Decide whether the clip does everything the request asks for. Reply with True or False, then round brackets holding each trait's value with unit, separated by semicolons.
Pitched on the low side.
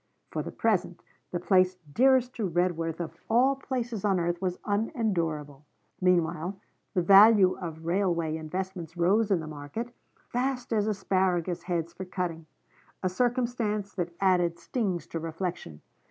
False (185 Hz)